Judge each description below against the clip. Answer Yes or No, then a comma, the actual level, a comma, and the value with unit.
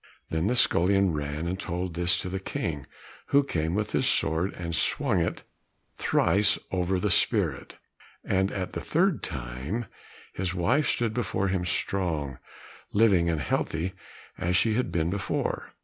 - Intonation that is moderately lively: Yes, average, 3.4 semitones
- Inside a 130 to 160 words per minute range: Yes, average, 155 wpm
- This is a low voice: Yes, very low, 90 Hz